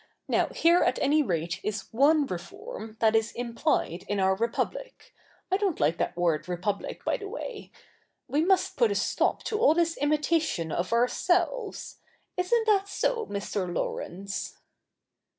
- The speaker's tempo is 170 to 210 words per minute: No, average, 160 wpm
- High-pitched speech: Yes, very high, 275 Hz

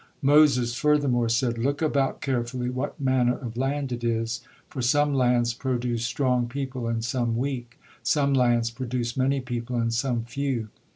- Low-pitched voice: Yes, low, 125 Hz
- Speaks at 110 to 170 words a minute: Yes, average, 160 wpm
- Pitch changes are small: Yes, narrow, 2.3 semitones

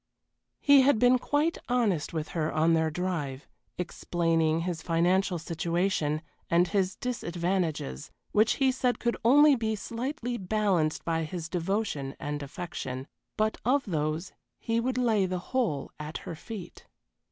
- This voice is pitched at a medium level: Yes, medium, 180 Hz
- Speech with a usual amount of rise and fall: No, wide, 6.0 semitones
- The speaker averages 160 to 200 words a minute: No, average, 140 wpm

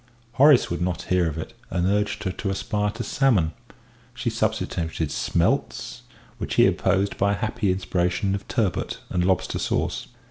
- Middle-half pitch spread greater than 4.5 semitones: No, average, 2.8 semitones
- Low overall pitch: Yes, very low, 95 Hz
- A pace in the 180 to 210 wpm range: No, average, 165 wpm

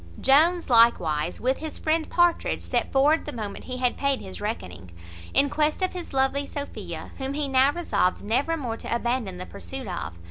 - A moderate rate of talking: Yes, average, 185 wpm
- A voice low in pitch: No, very high, 265 Hz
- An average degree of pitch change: Yes, average, 4.9 semitones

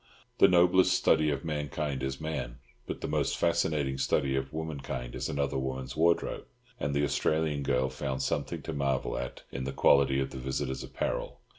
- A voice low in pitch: Yes, very low, 70 Hz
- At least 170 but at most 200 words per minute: Yes, average, 175 wpm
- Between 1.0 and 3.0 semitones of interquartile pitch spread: Yes, average, 2.7 semitones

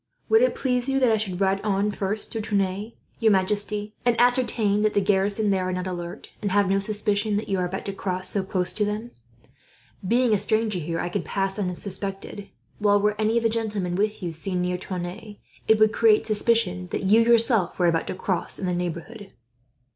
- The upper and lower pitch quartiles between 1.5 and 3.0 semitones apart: Yes, average, 2.7 semitones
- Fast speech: Yes, fast, 210 wpm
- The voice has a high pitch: Yes, high, 205 Hz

